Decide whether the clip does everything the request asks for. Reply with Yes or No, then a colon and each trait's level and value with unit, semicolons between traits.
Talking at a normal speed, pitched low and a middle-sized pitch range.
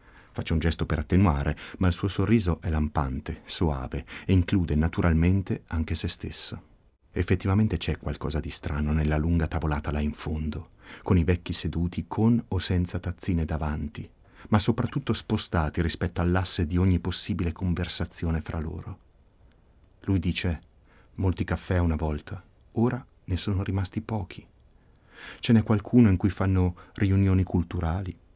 Yes: average, 145 wpm; very low, 90 Hz; average, 3.5 semitones